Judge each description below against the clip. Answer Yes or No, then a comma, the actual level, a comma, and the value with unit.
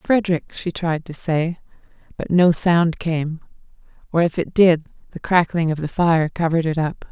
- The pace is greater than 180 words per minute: No, average, 175 wpm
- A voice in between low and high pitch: Yes, medium, 165 Hz